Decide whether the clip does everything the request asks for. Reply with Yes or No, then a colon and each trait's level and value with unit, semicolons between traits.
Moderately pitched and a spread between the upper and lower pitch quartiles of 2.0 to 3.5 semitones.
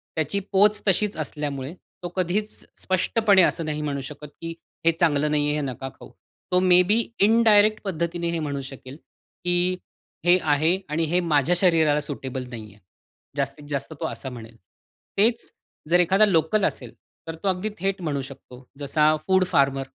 No: medium, 160 Hz; average, 4.7 semitones